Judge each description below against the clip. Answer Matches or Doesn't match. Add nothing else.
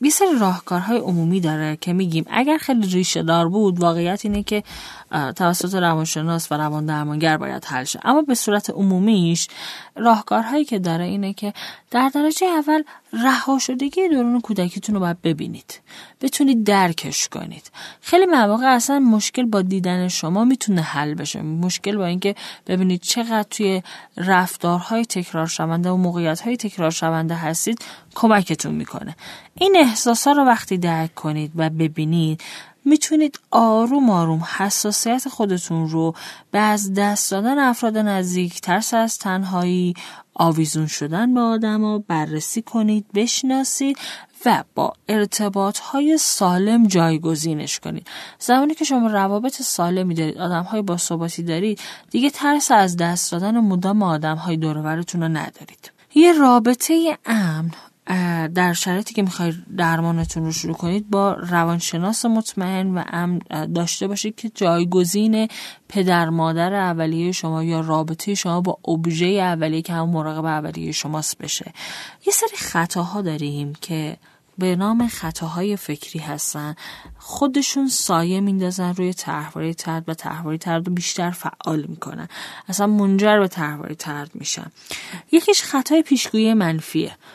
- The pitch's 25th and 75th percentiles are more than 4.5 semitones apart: Matches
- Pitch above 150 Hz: Matches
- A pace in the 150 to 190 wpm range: Doesn't match